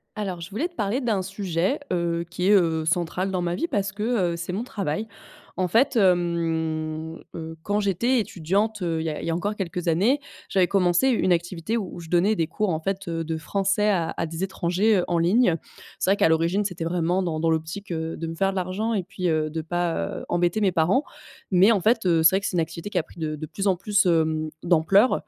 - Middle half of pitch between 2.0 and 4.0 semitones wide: Yes, average, 3.4 semitones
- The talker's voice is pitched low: No, medium, 180 Hz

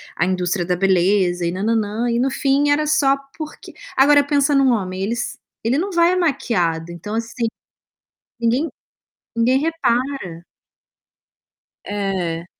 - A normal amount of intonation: No, wide, 7.1 semitones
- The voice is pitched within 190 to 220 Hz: No, high, 230 Hz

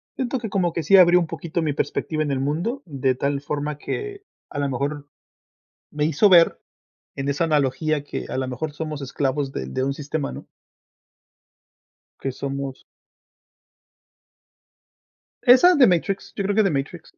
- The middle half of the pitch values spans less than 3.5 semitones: No, average, 4.2 semitones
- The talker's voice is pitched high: No, medium, 150 Hz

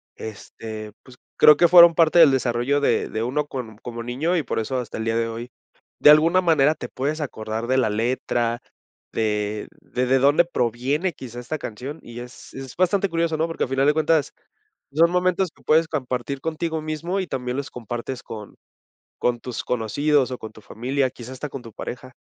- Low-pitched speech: Yes, low, 130 Hz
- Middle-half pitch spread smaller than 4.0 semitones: No, average, 4.8 semitones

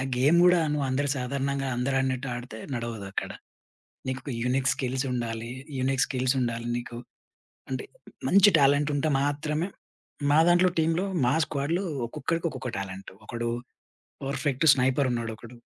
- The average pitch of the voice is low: Yes, low, 130 Hz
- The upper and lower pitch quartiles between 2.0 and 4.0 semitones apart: Yes, average, 2.9 semitones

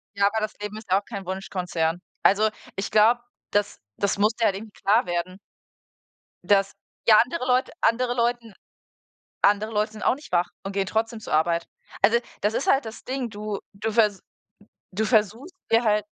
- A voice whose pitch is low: No, high, 210 Hz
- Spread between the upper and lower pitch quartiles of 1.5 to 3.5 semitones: Yes, narrow, 2.6 semitones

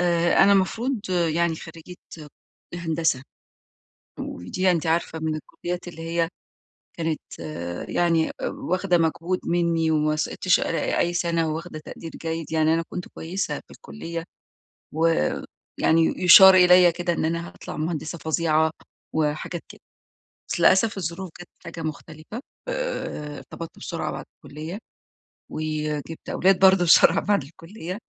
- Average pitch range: No, narrow, 1.9 semitones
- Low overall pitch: No, medium, 165 Hz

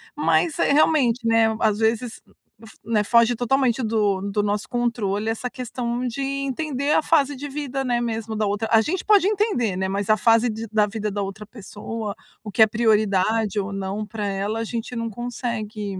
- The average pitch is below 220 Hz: No, high, 225 Hz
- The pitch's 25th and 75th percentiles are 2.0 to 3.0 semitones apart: Yes, average, 2.7 semitones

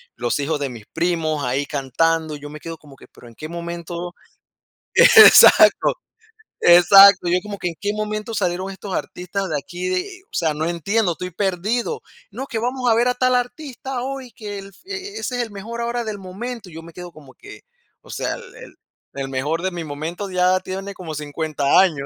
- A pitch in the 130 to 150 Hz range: No, medium, 180 Hz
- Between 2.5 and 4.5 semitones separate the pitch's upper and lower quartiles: No, wide, 5.6 semitones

